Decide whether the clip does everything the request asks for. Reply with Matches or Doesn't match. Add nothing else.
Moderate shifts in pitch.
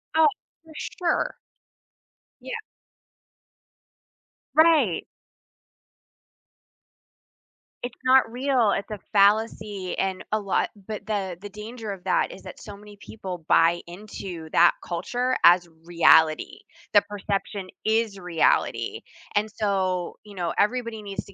Matches